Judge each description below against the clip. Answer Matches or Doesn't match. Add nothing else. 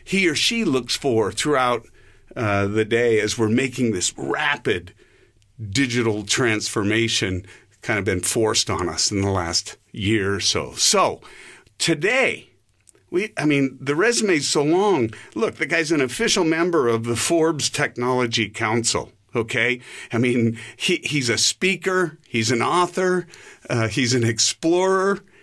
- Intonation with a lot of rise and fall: Matches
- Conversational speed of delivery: Matches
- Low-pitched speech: Matches